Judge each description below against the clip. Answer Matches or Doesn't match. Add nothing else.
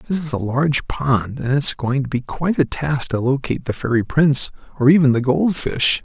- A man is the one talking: Matches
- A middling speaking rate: Doesn't match